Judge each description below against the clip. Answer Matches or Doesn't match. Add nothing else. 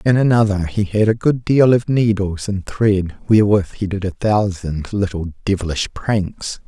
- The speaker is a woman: Doesn't match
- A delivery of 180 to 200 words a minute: Doesn't match